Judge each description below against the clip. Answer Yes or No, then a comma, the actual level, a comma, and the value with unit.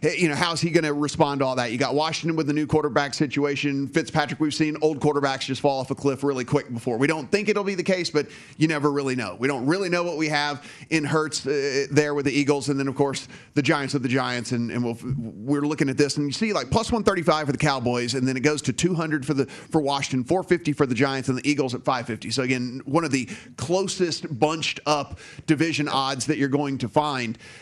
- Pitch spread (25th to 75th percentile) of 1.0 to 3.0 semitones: Yes, average, 2.7 semitones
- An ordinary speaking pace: No, fast, 260 wpm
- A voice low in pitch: No, medium, 145 Hz